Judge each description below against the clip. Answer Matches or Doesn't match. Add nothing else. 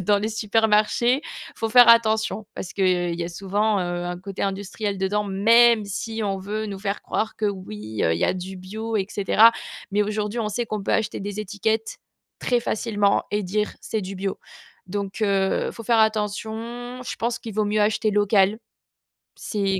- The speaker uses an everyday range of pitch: Doesn't match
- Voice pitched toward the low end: Doesn't match